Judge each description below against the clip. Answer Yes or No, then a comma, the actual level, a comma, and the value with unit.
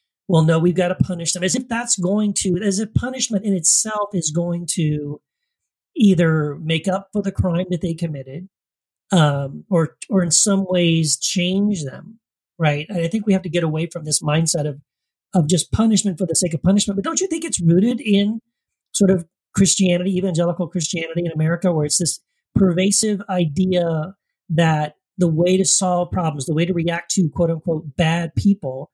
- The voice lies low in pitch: No, medium, 175 Hz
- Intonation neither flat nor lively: Yes, average, 3.1 semitones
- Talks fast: No, average, 190 wpm